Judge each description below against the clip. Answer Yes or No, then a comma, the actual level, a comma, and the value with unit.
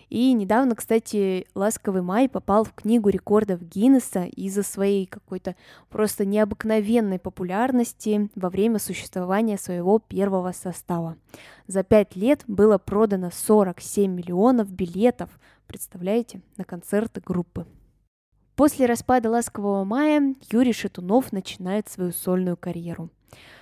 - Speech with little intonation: No, average, 3.3 semitones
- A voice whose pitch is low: No, high, 205 Hz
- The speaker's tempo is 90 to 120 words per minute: Yes, slow, 110 wpm